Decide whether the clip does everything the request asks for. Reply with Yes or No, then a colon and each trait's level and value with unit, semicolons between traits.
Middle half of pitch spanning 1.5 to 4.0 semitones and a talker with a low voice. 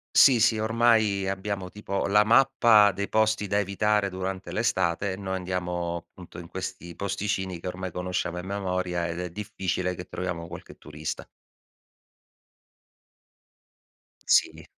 Yes: narrow, 2.5 semitones; very low, 95 Hz